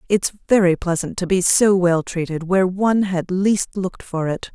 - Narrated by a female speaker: Yes, female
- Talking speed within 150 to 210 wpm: Yes, average, 200 wpm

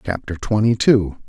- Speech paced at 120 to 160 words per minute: Yes, average, 140 wpm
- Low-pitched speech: Yes, low, 105 Hz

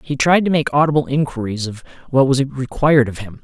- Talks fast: Yes, fast, 210 wpm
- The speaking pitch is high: No, low, 135 Hz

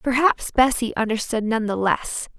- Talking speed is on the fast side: No, average, 150 wpm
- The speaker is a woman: Yes, female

